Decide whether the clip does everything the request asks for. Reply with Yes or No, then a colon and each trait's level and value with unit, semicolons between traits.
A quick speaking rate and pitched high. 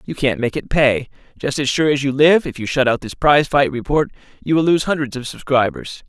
No: fast, 245 wpm; medium, 140 Hz